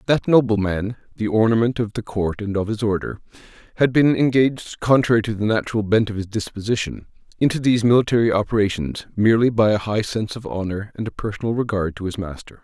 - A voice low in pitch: Yes, low, 110 Hz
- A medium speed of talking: Yes, average, 190 wpm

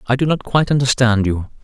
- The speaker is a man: Yes, male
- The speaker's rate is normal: No, fast, 220 wpm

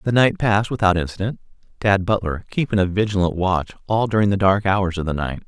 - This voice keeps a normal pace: No, fast, 210 wpm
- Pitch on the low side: Yes, low, 100 Hz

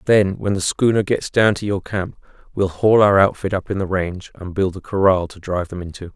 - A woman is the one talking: No, male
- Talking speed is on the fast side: Yes, fast, 245 wpm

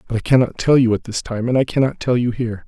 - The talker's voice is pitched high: No, low, 120 Hz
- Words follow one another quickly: Yes, fast, 315 wpm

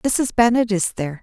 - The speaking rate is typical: Yes, average, 195 wpm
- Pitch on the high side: Yes, high, 215 Hz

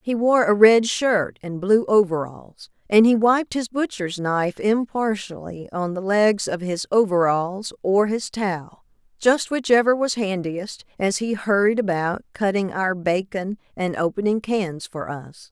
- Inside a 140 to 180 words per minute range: Yes, average, 150 wpm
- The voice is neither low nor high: No, high, 200 Hz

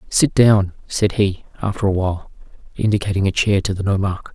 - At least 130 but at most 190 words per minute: Yes, average, 180 wpm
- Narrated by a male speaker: Yes, male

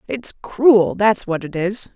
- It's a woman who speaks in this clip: Yes, female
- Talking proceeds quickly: No, average, 185 wpm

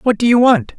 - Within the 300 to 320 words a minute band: Yes, fast, 305 wpm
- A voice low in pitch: No, high, 225 Hz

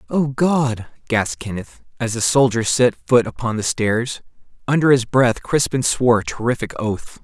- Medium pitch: No, low, 120 Hz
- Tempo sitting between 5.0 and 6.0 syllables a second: No, 4.7 syllables/s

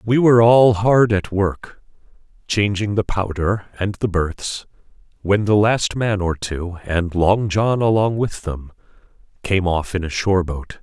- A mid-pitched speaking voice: No, low, 100 Hz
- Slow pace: No, average, 165 wpm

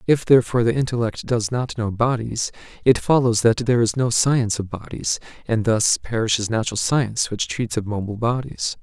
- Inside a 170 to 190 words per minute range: Yes, average, 185 wpm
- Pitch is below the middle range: Yes, low, 115 Hz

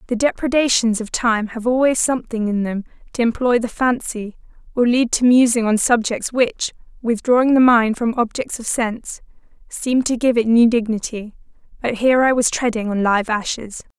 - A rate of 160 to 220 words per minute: Yes, average, 175 wpm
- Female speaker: Yes, female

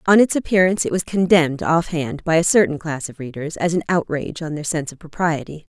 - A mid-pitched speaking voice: Yes, medium, 165 Hz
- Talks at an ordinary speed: No, fast, 230 wpm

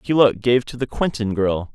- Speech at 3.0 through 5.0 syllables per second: Yes, 4.7 syllables/s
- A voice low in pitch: Yes, low, 115 Hz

